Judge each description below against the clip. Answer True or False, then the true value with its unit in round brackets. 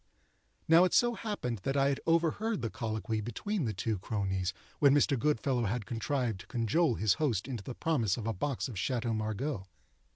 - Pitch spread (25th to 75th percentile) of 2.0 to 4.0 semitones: False (5.1 semitones)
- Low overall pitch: True (120 Hz)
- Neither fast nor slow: True (190 wpm)